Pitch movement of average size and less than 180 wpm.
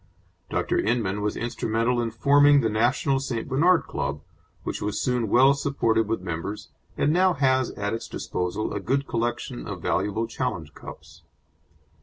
Yes: average, 4.4 semitones; average, 155 wpm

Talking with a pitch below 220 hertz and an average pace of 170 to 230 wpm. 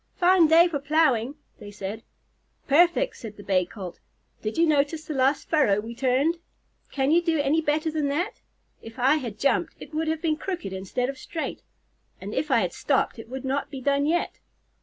No: very high, 280 Hz; average, 200 wpm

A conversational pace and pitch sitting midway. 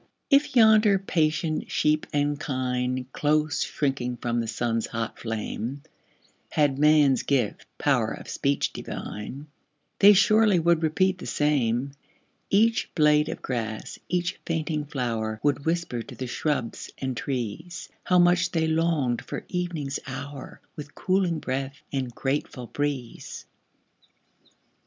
No: slow, 130 wpm; medium, 145 Hz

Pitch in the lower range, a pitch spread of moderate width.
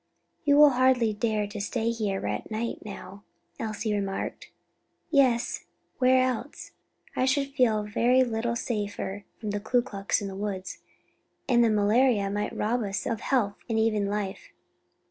No: high, 220 Hz; average, 3.3 semitones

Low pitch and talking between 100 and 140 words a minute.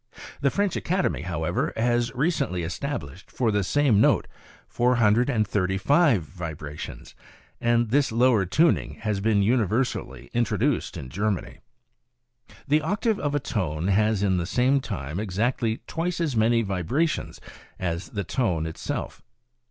Yes: low, 110 Hz; slow, 135 wpm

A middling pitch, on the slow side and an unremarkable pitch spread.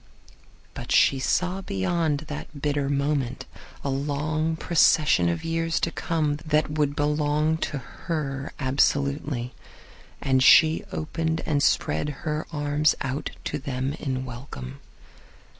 No: medium, 145 Hz; slow, 125 wpm; narrow, 2.3 semitones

